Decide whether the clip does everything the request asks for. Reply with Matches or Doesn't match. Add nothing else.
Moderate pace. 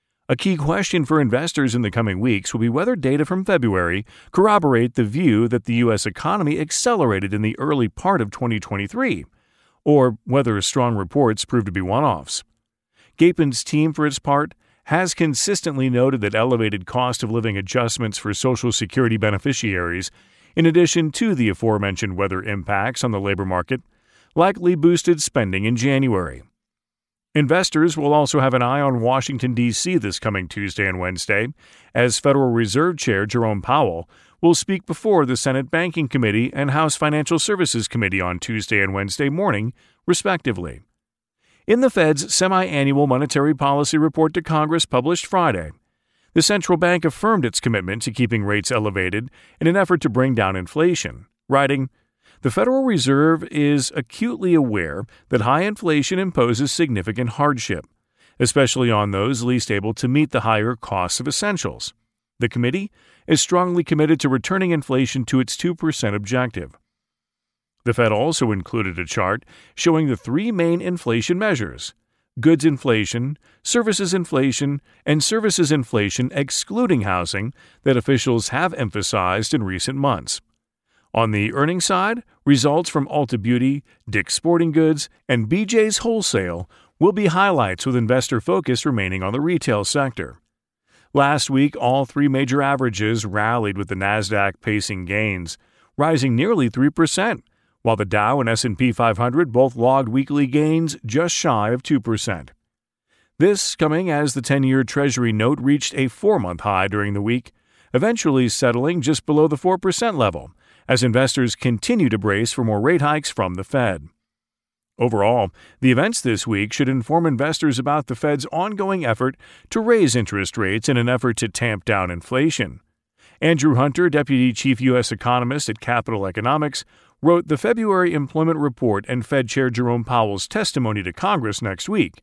Matches